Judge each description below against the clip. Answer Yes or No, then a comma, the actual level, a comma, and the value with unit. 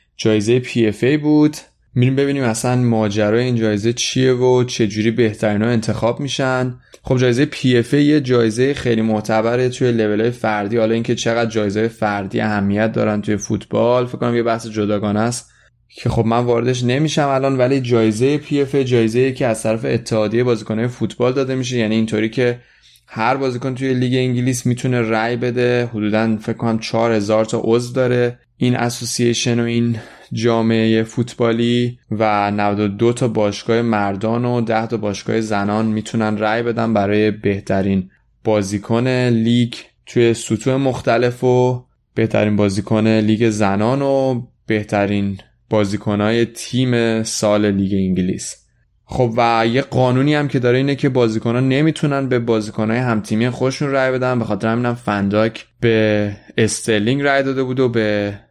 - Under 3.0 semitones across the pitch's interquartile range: Yes, narrow, 2.4 semitones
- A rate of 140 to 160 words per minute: Yes, average, 150 wpm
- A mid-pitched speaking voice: No, low, 115 Hz